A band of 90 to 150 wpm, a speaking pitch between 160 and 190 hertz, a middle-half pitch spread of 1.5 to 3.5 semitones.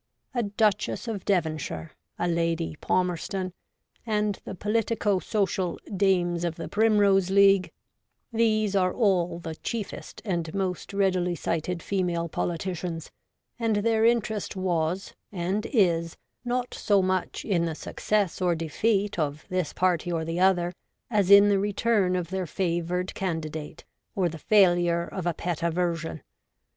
Yes: average, 140 wpm; medium, 185 Hz; average, 3.1 semitones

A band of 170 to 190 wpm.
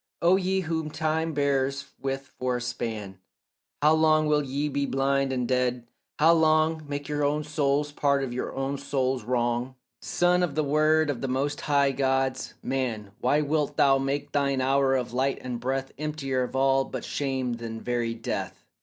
Yes: average, 185 wpm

